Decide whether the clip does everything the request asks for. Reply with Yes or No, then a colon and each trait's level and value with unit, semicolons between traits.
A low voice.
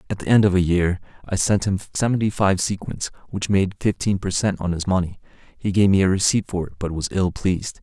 Yes: very low, 95 Hz